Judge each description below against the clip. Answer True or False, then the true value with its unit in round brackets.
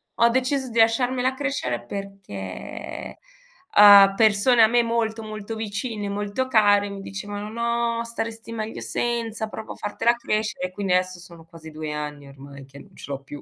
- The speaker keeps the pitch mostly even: False (4.1 semitones)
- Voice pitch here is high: True (210 Hz)